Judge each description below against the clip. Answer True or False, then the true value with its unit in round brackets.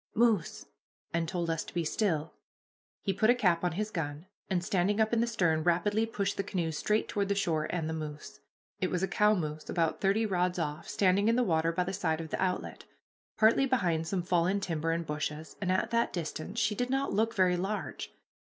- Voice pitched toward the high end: False (180 Hz)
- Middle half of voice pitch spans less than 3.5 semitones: False (4.2 semitones)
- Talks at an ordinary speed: False (220 wpm)